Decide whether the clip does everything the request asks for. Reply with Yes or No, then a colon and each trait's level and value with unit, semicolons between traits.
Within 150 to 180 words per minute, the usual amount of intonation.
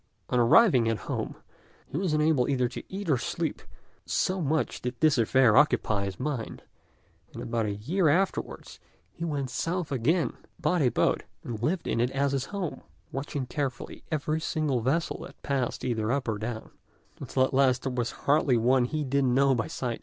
No: average, 190 wpm; average, 4.1 semitones